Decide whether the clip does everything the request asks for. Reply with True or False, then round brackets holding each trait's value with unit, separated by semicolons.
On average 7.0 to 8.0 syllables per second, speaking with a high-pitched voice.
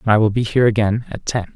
False (7.3 syllables/s; 110 Hz)